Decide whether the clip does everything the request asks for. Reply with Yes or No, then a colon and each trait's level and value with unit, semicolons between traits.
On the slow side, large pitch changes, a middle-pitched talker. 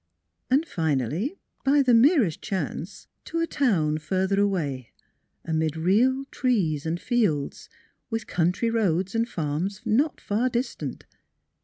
No: slow, 125 wpm; wide, 7.3 semitones; high, 195 Hz